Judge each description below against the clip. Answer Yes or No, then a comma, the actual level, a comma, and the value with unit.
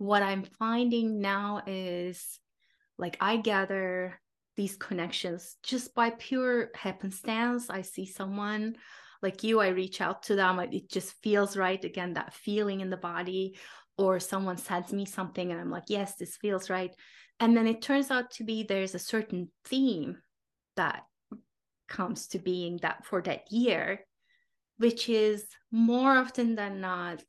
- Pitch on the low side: No, high, 200 Hz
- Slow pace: No, average, 160 wpm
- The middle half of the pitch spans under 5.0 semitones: Yes, average, 3.7 semitones